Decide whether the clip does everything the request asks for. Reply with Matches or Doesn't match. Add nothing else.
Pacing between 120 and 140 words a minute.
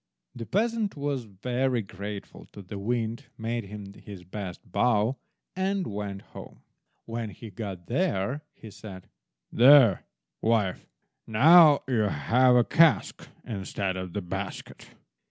Matches